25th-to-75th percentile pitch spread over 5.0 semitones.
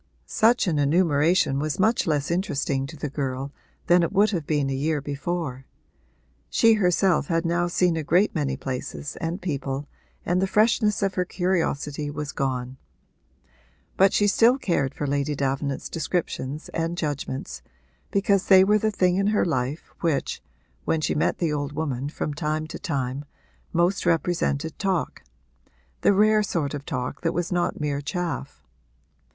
No: average, 4.4 semitones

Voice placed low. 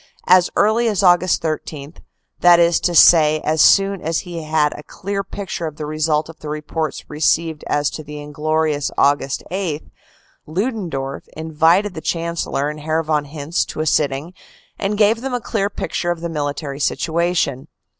No: medium, 160 Hz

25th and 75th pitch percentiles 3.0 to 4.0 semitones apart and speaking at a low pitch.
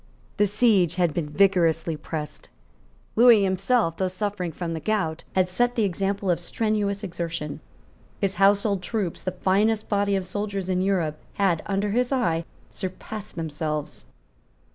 No: average, 3.4 semitones; high, 190 Hz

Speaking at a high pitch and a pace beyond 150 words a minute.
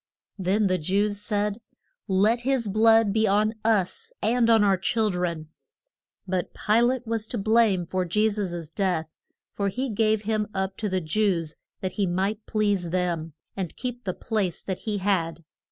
Yes: high, 205 Hz; average, 170 wpm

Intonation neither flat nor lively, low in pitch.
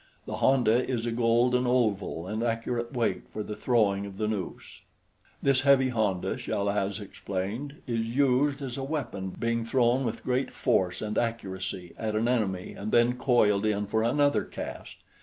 Yes: average, 3.3 semitones; low, 115 Hz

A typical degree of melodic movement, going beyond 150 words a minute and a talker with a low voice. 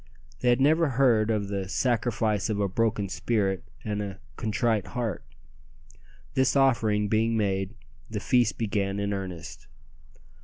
No: average, 3.0 semitones; average, 140 wpm; low, 110 Hz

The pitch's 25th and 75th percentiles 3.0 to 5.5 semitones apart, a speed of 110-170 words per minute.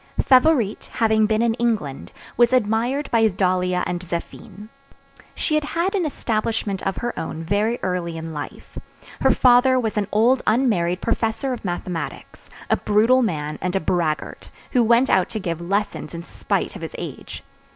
Yes: average, 5.0 semitones; average, 165 wpm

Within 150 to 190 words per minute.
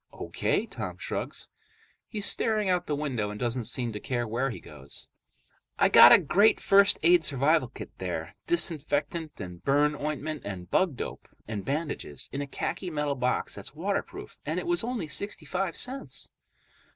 Yes: average, 170 wpm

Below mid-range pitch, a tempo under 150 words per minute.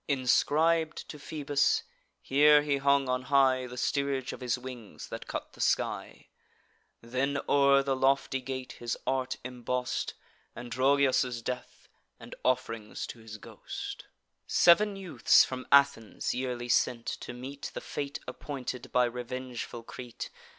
Yes: low, 130 Hz; slow, 135 wpm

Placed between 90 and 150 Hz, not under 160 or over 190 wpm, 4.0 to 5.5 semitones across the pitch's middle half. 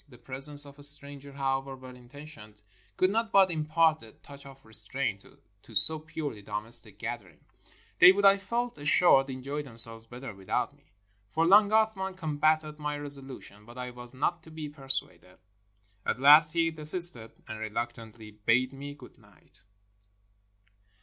Yes: medium, 140 Hz; average, 165 wpm; average, 4.7 semitones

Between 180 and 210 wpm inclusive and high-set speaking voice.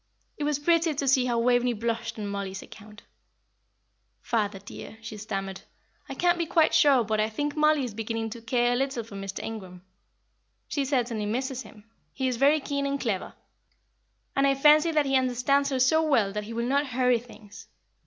Yes: average, 195 wpm; high, 245 Hz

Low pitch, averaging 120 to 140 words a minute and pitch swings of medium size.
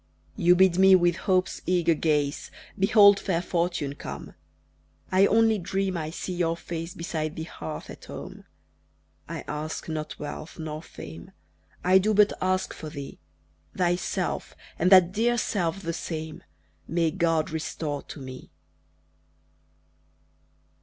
No: medium, 170 Hz; slow, 135 wpm; average, 3.2 semitones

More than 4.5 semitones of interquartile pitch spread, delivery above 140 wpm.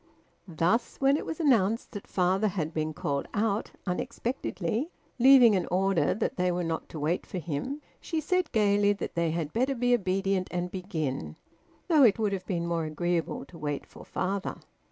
Yes: average, 5.3 semitones; average, 180 wpm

